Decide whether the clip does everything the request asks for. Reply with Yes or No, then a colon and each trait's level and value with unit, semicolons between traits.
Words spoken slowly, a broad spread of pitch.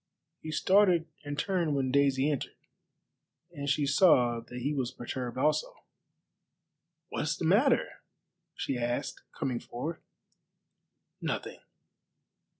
No: slow, 115 wpm; average, 3.7 semitones